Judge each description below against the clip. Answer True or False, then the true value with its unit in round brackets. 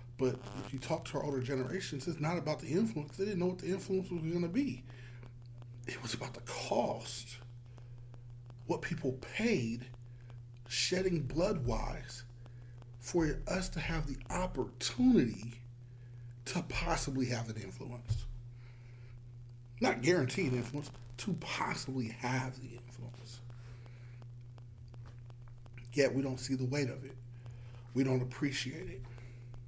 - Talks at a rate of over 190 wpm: False (135 wpm)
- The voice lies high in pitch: False (125 Hz)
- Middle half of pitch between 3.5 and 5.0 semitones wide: False (2.9 semitones)